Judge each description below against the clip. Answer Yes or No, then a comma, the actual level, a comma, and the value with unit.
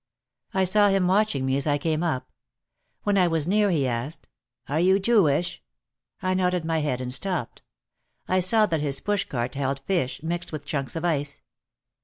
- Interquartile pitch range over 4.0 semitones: Yes, average, 5.1 semitones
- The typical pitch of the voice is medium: Yes, medium, 165 Hz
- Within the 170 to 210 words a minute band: Yes, average, 185 wpm